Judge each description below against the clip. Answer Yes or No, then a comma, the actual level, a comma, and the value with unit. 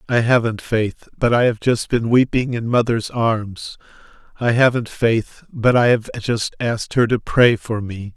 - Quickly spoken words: No, average, 185 wpm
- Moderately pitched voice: No, low, 115 Hz